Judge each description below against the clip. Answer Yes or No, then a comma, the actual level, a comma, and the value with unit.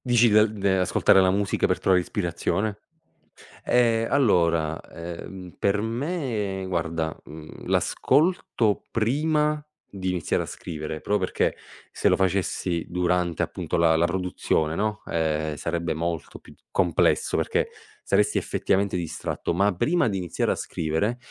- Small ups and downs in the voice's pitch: No, average, 4.4 semitones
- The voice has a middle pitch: No, very low, 95 Hz